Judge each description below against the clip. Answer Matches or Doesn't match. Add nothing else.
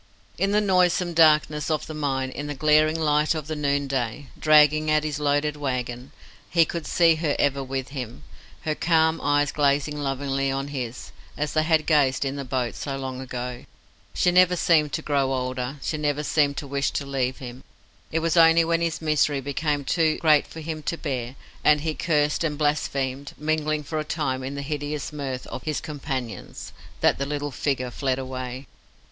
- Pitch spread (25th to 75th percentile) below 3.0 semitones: Matches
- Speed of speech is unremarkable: Matches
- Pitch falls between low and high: Matches